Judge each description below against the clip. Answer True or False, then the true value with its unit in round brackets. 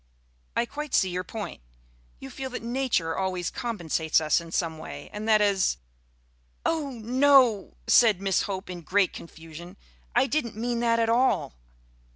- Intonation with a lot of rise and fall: True (5.8 semitones)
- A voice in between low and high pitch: False (205 Hz)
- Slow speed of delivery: False (165 wpm)